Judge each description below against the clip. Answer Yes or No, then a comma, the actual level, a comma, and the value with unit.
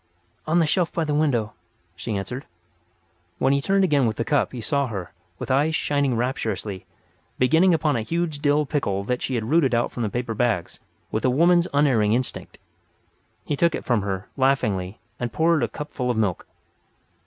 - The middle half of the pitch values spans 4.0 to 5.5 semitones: Yes, average, 5.2 semitones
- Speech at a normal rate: Yes, average, 190 wpm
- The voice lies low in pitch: Yes, low, 130 Hz